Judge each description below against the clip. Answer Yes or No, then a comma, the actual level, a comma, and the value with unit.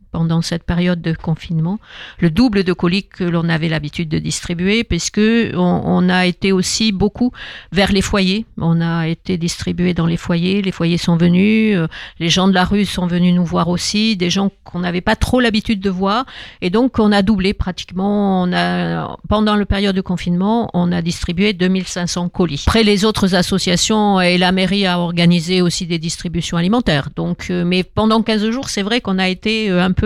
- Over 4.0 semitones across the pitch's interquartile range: No, average, 2.9 semitones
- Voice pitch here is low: No, medium, 185 Hz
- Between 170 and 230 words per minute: Yes, average, 195 wpm